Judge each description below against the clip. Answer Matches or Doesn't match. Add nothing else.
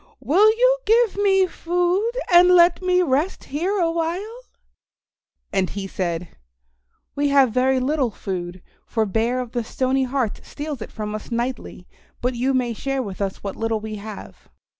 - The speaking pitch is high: Matches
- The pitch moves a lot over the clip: Matches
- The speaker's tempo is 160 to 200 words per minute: Matches